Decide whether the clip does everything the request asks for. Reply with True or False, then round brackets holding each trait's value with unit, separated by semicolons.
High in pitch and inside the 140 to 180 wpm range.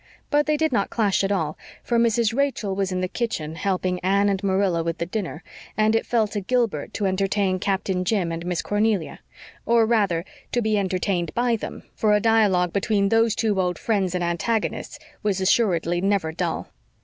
False (200 Hz; 190 wpm)